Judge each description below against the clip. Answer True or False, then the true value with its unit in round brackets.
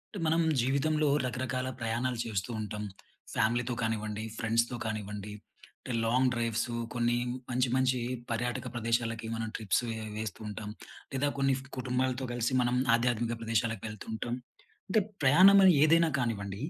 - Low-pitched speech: True (120 Hz)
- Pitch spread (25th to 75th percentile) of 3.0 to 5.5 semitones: False (2.5 semitones)